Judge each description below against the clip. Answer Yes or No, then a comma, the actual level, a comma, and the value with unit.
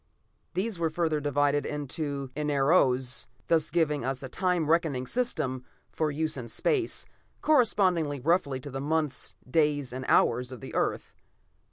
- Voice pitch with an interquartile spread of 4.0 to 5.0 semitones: No, average, 3.6 semitones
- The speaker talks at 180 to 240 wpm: No, average, 145 wpm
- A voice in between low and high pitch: Yes, medium, 150 Hz